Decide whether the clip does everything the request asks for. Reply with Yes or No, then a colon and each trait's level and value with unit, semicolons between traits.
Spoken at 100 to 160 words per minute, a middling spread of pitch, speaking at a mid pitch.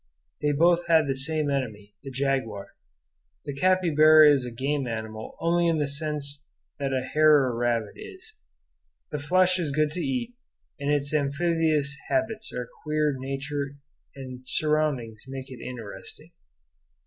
Yes: average, 150 wpm; average, 3.0 semitones; medium, 145 Hz